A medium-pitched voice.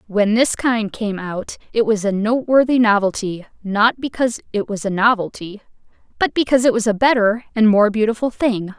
No: high, 220 Hz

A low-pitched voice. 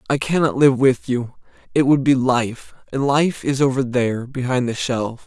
Yes: low, 130 Hz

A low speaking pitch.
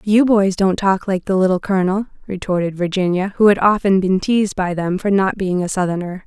No: high, 190 Hz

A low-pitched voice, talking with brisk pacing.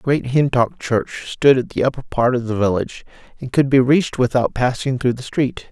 Yes: low, 125 Hz; fast, 210 wpm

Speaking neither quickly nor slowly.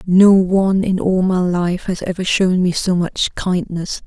Yes: average, 190 wpm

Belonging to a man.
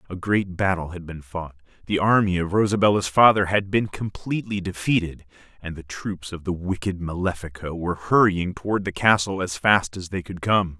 Yes: male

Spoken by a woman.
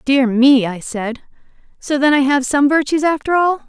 Yes: female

